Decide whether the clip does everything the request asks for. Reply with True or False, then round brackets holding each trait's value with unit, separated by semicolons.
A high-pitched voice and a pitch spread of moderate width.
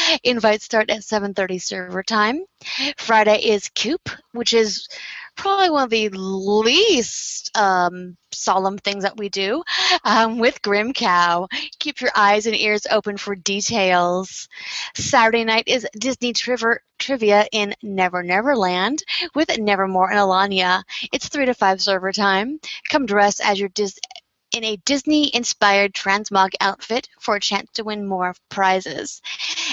True (210 Hz; 4.1 semitones)